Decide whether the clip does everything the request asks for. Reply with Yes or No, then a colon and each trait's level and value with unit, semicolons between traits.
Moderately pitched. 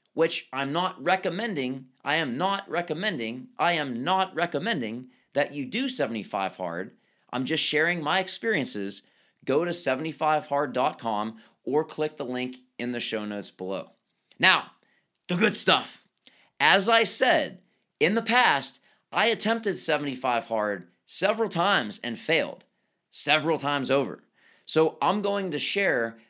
Yes: medium, 155 Hz